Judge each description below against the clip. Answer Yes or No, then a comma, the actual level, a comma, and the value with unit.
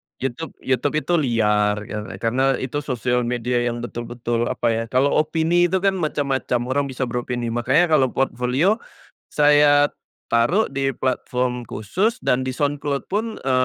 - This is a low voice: Yes, low, 130 Hz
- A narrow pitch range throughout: No, average, 3.4 semitones